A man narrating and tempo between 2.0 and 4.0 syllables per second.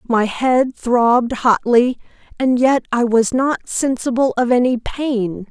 No: female; 3.8 syllables/s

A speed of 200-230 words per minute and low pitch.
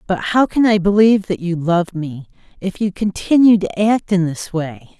No: fast, 205 wpm; high, 190 Hz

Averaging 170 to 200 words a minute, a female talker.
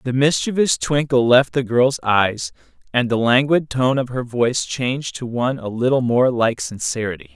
No: average, 180 wpm; male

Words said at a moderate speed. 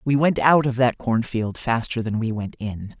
No: fast, 220 wpm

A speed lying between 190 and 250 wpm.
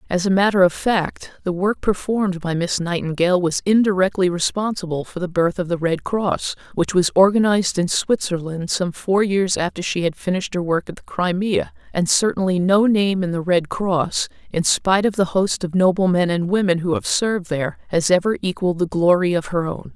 Yes: fast, 205 wpm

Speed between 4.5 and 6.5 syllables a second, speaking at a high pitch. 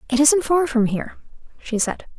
Yes: 5.3 syllables/s; very high, 270 Hz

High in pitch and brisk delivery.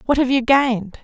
Yes: very high, 250 Hz; fast, 235 wpm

